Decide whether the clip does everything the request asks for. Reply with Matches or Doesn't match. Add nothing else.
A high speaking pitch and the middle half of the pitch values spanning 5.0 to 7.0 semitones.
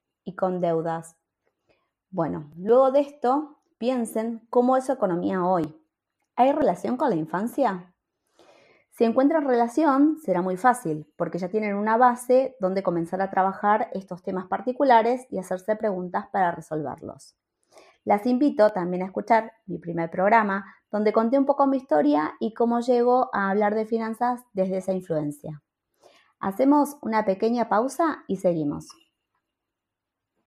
Matches